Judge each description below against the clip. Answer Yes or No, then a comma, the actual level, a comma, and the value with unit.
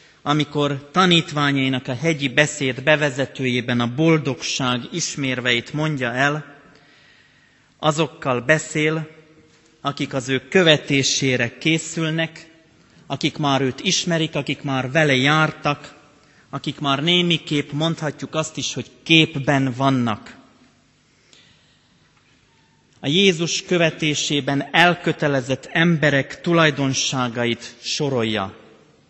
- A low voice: No, medium, 145 Hz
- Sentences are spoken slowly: Yes, slow, 90 wpm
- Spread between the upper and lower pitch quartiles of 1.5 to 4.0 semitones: Yes, average, 2.9 semitones